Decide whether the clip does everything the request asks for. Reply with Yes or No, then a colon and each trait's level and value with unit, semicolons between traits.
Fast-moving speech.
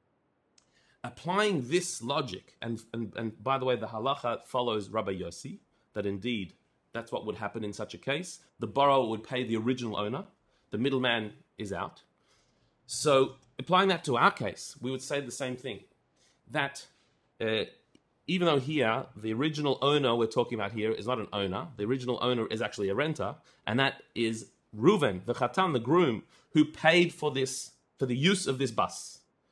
No: average, 180 wpm